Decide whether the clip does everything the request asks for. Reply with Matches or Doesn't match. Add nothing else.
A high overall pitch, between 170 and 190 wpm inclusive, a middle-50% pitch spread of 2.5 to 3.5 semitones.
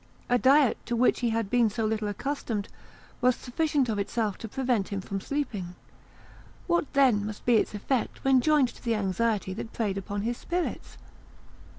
Doesn't match